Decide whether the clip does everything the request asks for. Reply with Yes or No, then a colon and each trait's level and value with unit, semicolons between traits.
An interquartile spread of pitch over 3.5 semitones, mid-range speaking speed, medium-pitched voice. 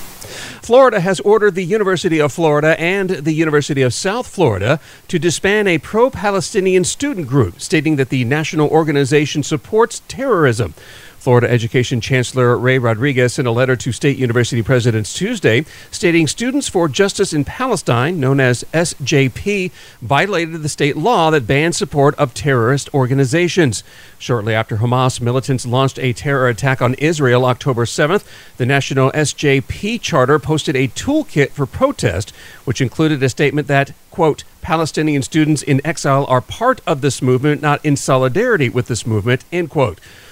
Yes: average, 4.7 semitones; average, 155 wpm; medium, 145 Hz